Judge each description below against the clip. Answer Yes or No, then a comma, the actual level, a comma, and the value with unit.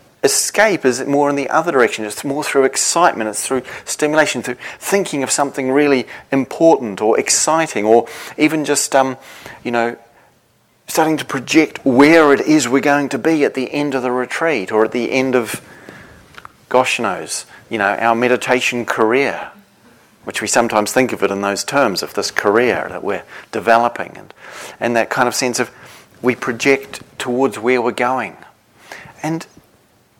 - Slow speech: No, average, 170 wpm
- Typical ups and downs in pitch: Yes, average, 3.3 semitones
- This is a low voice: Yes, low, 130 Hz